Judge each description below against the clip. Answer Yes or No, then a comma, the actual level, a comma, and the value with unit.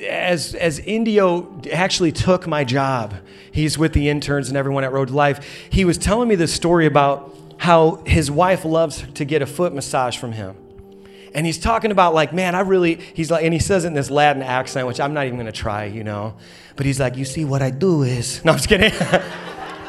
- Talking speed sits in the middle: No, fast, 225 wpm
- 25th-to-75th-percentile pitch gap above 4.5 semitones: Yes, average, 4.9 semitones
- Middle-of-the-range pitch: Yes, medium, 145 Hz